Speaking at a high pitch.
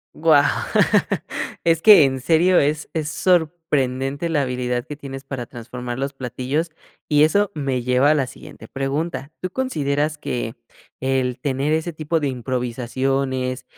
No: medium, 140 Hz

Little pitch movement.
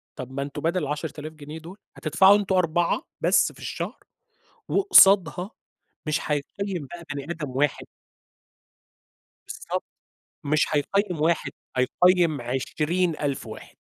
No: average, 3.8 semitones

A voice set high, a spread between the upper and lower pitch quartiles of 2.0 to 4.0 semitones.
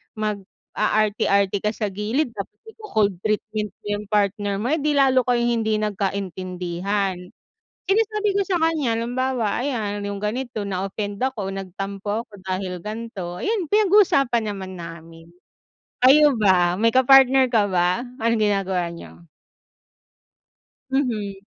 No: high, 210 Hz; average, 4.5 semitones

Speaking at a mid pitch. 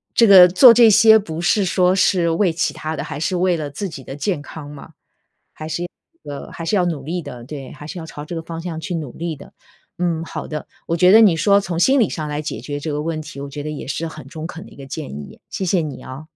Yes: medium, 165 Hz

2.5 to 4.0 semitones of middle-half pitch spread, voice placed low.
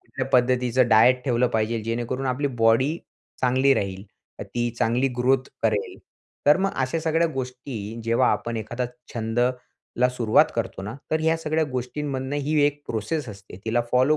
Yes: average, 2.9 semitones; low, 125 Hz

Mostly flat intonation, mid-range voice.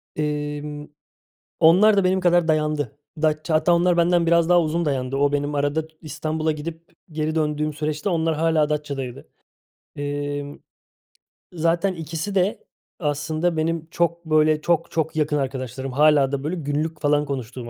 Yes: narrow, 2.3 semitones; medium, 155 Hz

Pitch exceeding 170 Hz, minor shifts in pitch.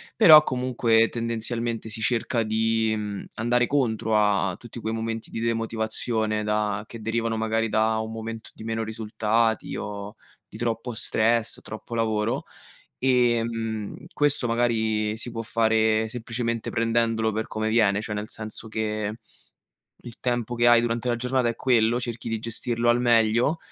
No: low, 115 Hz; narrow, 1.2 semitones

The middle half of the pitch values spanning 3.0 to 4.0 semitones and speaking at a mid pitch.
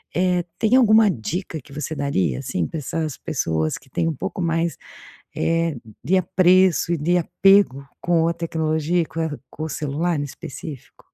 Yes: average, 3.6 semitones; medium, 165 Hz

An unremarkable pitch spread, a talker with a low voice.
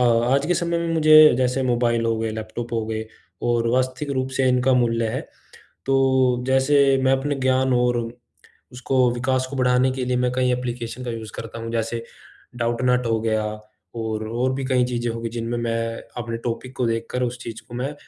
No: narrow, 2.0 semitones; low, 125 Hz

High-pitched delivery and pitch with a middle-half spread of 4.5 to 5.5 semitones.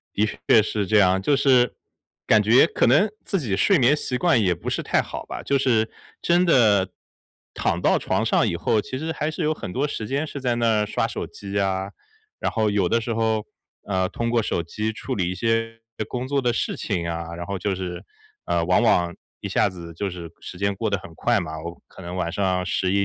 No: low, 105 Hz; average, 4.8 semitones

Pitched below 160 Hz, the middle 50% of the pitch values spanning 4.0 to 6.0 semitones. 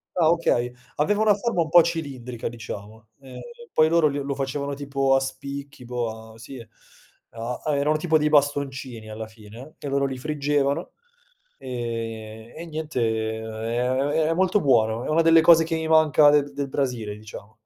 Yes: medium, 140 Hz; average, 5.0 semitones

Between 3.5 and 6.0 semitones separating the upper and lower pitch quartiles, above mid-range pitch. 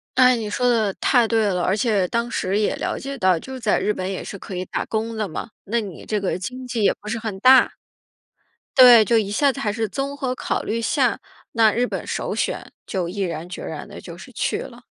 Yes: average, 3.9 semitones; high, 220 Hz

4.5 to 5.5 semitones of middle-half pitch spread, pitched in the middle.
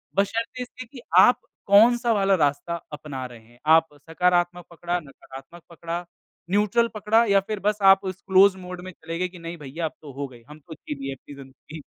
Yes: average, 5.0 semitones; medium, 175 Hz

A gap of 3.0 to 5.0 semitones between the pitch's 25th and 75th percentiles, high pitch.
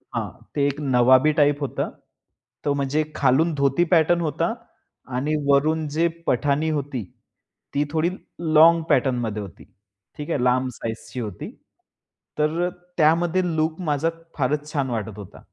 No: average, 3.5 semitones; medium, 145 Hz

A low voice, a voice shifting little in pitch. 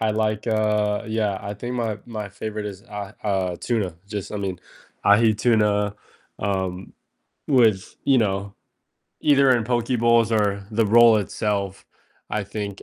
Yes: low, 105 Hz; narrow, 2.0 semitones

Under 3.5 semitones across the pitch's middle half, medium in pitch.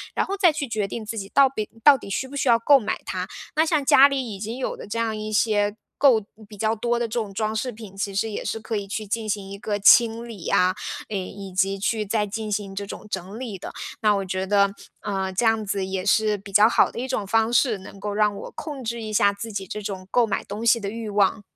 No: narrow, 2.6 semitones; high, 215 Hz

